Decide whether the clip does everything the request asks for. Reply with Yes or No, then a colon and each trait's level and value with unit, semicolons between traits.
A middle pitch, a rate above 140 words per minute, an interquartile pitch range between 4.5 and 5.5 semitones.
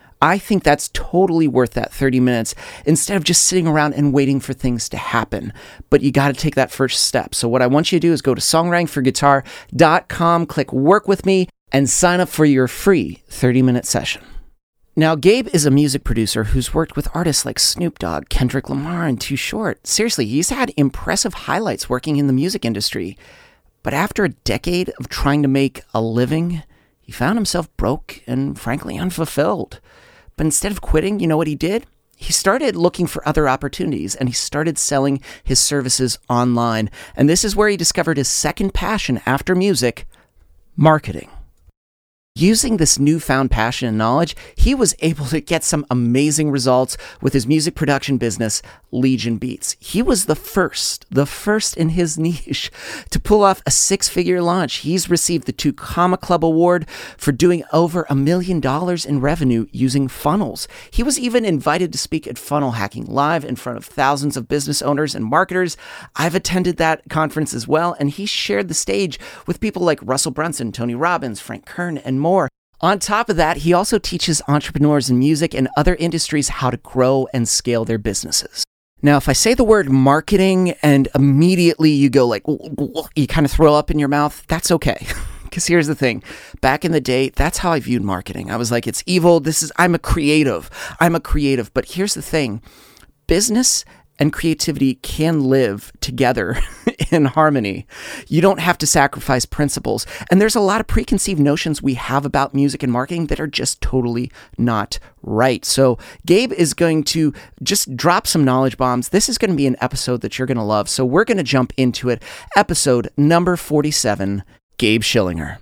Yes: medium, 145 Hz; average, 190 wpm; average, 5.1 semitones